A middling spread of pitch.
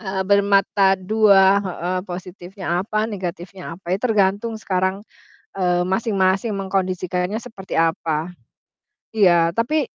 No: narrow, 2.0 semitones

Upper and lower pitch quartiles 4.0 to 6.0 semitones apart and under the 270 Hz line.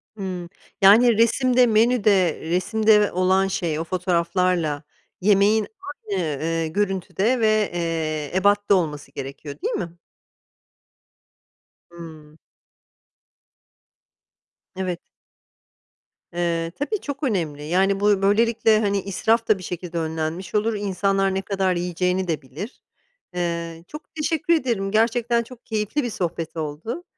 Yes: average, 4.4 semitones; high, 190 Hz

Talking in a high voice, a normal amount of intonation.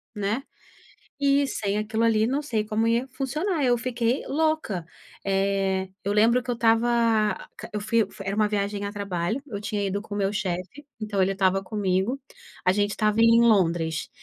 Yes: high, 210 Hz; average, 3.1 semitones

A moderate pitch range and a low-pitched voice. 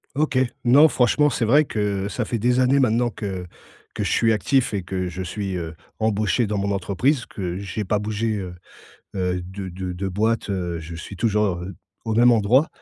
Yes: average, 4.0 semitones; low, 105 Hz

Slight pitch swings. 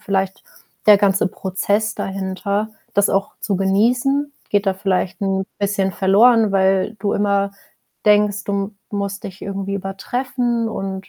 Yes: narrow, 1.5 semitones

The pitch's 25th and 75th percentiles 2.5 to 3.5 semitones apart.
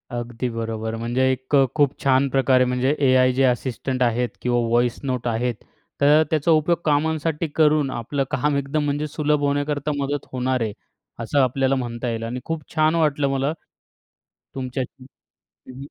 Yes: average, 2.9 semitones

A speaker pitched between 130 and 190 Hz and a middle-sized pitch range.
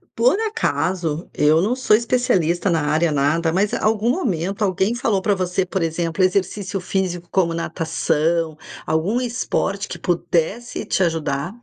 Yes: medium, 185 Hz; average, 4.1 semitones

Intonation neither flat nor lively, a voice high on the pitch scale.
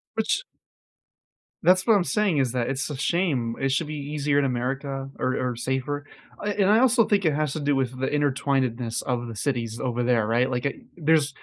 No: average, 3.5 semitones; low, 135 Hz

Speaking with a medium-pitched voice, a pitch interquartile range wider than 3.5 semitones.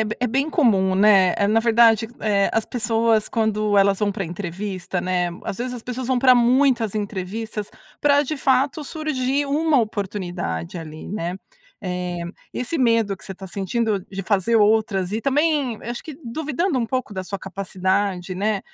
No: high, 215 Hz; average, 4.6 semitones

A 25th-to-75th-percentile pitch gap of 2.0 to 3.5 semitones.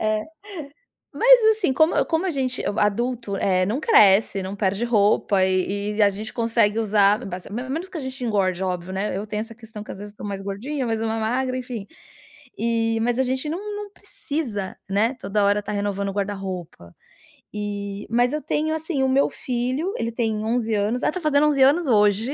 No: average, 4.4 semitones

